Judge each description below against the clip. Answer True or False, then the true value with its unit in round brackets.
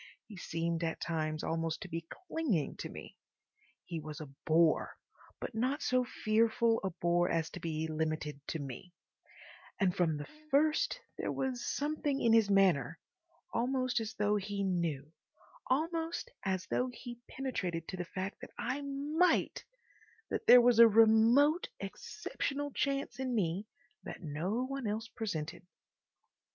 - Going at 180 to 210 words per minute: False (145 wpm)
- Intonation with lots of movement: True (7.9 semitones)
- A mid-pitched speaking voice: False (210 Hz)